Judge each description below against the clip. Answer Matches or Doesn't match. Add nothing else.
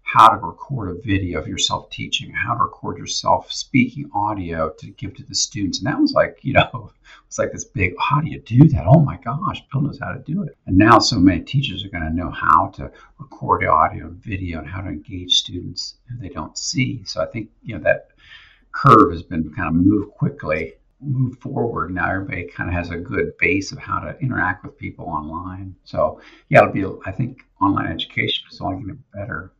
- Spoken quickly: Matches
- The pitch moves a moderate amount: Doesn't match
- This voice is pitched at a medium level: Doesn't match